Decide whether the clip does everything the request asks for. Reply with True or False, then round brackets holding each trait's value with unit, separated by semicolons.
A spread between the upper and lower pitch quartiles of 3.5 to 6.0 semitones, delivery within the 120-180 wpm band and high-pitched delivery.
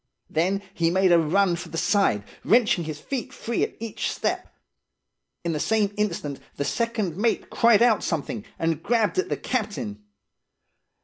True (5.4 semitones; 165 wpm; 195 Hz)